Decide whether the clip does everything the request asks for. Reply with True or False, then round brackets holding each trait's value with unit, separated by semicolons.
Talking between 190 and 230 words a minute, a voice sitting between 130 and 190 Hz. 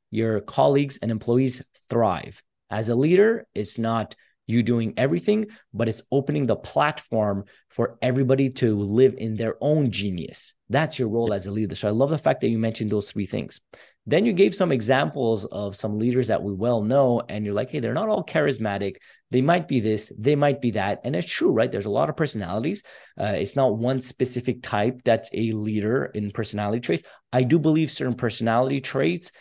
False (200 wpm; 120 Hz)